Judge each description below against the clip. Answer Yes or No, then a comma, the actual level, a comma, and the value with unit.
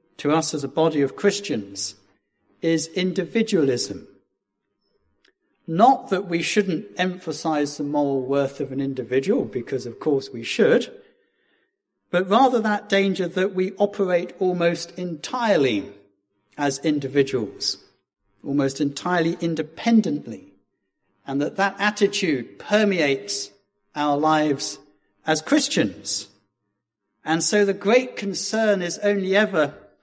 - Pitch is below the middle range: No, medium, 165 Hz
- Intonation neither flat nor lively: No, wide, 6.4 semitones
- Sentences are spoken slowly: Yes, slow, 110 wpm